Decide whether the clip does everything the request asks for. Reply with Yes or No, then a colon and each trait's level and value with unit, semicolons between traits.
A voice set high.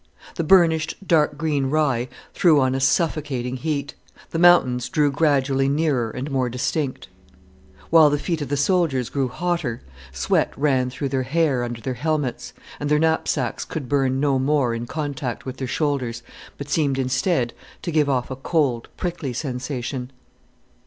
No: medium, 140 Hz